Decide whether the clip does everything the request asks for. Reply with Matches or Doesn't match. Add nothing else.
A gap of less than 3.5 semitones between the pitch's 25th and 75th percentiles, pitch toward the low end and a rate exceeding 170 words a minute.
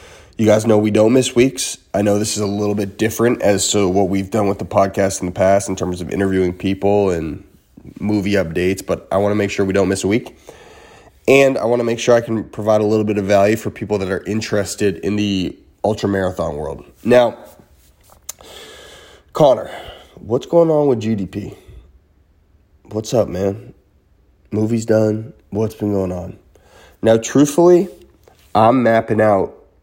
Matches